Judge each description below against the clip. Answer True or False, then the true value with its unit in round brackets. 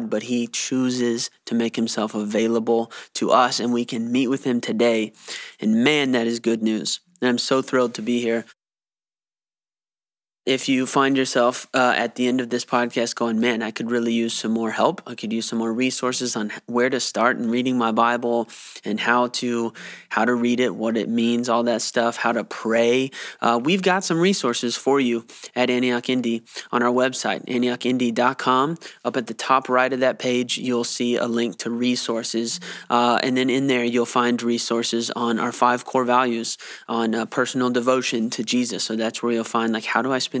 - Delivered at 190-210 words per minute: True (200 wpm)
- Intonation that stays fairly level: True (1.6 semitones)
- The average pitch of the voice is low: True (120 Hz)